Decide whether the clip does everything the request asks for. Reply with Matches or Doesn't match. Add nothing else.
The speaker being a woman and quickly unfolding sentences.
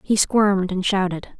Doesn't match